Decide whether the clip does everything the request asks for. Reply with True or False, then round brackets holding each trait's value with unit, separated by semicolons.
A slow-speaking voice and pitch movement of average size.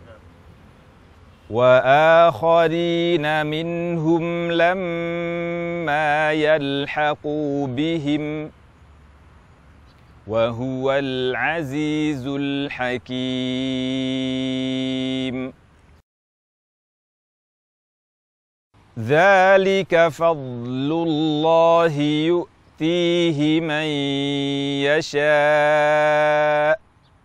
True (30 wpm; 4.2 semitones)